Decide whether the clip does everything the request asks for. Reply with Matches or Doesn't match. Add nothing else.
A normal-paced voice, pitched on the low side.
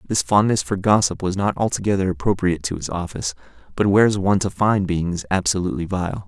Matches